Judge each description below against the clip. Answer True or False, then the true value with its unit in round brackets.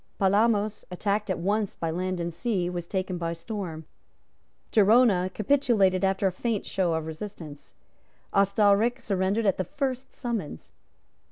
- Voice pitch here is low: False (195 Hz)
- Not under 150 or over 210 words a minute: False (140 wpm)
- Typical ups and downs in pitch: True (3.3 semitones)